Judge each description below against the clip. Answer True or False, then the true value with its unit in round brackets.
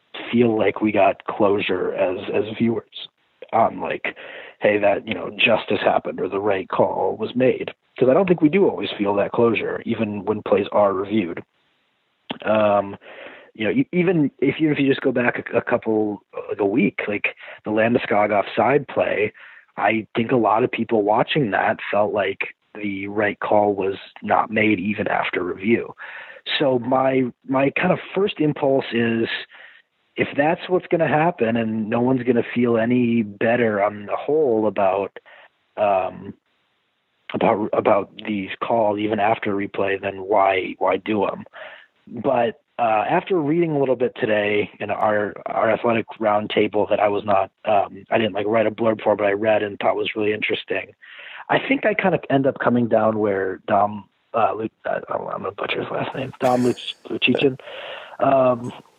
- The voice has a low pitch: True (115 Hz)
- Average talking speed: True (180 wpm)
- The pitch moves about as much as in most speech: True (4.4 semitones)